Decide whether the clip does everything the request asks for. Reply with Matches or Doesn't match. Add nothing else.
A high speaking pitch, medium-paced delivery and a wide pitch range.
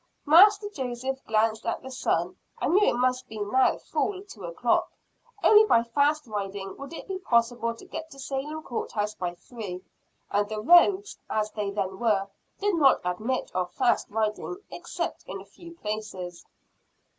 Matches